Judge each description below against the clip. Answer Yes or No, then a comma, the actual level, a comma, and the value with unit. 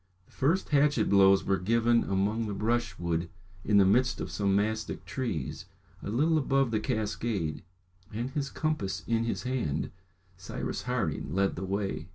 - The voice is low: Yes, low, 110 Hz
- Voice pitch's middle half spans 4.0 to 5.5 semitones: Yes, average, 4.4 semitones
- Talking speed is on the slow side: No, average, 160 wpm